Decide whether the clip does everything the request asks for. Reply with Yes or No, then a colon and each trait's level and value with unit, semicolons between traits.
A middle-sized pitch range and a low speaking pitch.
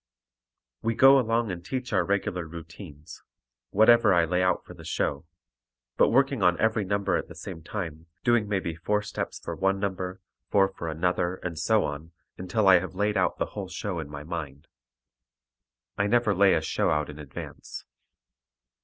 Yes: average, 3.9 semitones; very low, 95 Hz